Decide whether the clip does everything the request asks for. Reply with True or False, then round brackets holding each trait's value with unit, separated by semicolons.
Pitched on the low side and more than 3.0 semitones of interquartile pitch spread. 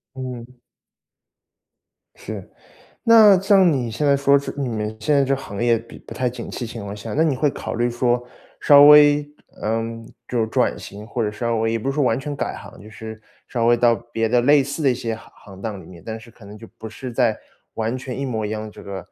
True (120 Hz; 3.7 semitones)